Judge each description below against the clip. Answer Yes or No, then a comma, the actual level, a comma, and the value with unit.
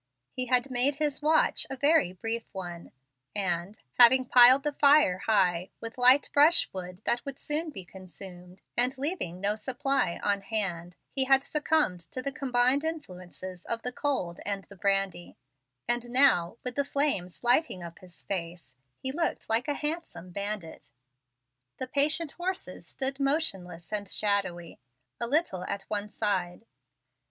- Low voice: No, high, 230 Hz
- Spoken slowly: No, average, 155 wpm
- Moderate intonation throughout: No, wide, 7.1 semitones